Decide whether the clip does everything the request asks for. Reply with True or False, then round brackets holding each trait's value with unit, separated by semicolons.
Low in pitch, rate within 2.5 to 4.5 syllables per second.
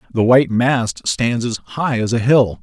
True (120 Hz; 4.4 syllables/s)